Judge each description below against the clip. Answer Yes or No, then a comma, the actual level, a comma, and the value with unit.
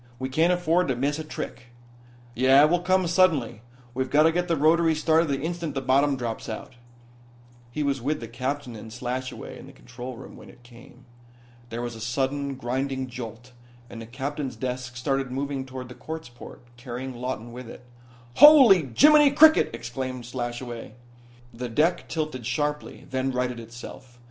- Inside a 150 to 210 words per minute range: Yes, average, 175 wpm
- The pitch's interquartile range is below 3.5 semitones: No, average, 3.8 semitones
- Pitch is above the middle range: No, low, 130 Hz